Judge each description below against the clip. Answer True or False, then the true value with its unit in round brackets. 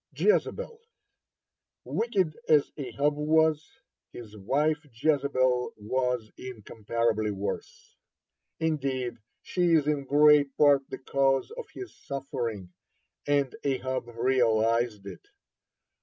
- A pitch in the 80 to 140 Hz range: True (135 Hz)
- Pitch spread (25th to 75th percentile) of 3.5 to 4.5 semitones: True (4.2 semitones)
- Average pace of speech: False (100 wpm)